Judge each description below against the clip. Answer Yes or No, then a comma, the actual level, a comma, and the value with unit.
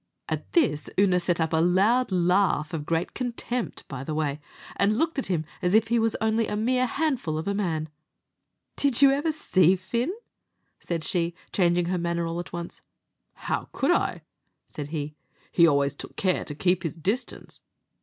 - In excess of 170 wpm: Yes, average, 185 wpm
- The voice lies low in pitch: No, medium, 180 Hz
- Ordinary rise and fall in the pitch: No, wide, 5.7 semitones